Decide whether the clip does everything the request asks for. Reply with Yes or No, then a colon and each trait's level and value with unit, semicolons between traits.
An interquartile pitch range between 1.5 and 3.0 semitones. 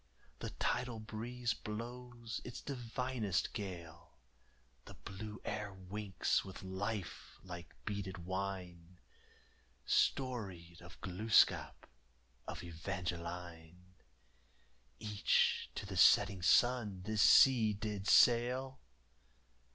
No: average, 4.2 semitones